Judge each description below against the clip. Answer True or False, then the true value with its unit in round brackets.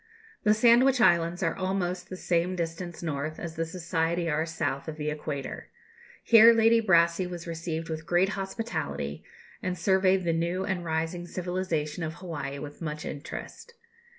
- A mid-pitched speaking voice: True (170 Hz)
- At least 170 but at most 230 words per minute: False (155 wpm)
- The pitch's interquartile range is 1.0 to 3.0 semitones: True (2.6 semitones)